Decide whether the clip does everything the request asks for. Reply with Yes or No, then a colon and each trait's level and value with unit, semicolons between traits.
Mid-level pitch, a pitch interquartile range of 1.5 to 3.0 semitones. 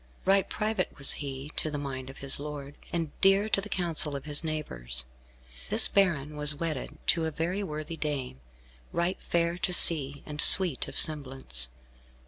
No: medium, 150 Hz; average, 3.7 semitones